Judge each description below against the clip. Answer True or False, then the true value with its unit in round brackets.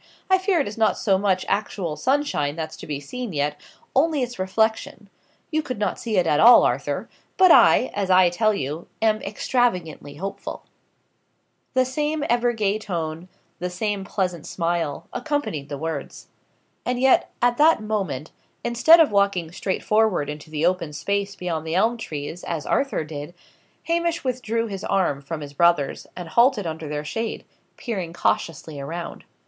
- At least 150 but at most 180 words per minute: True (165 wpm)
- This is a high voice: True (195 Hz)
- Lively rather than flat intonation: True (6.6 semitones)